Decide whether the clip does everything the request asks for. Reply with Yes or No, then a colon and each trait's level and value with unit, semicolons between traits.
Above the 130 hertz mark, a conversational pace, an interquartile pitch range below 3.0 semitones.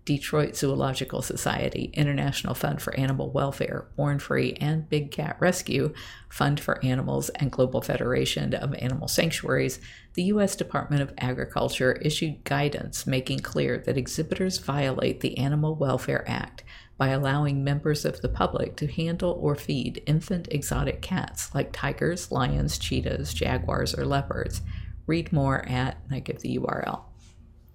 No: medium, 140 Hz; average, 145 wpm; average, 3.4 semitones